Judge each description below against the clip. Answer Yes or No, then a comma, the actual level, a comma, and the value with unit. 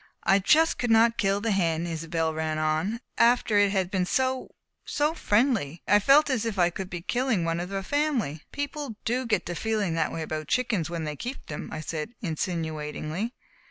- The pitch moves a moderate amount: No, wide, 6.4 semitones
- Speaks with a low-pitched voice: No, high, 195 Hz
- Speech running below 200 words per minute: No, fast, 205 wpm